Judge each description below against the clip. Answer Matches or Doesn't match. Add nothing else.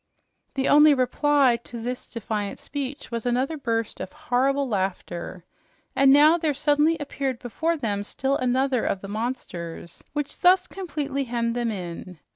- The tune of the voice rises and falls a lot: Doesn't match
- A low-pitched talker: Doesn't match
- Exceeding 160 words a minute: Doesn't match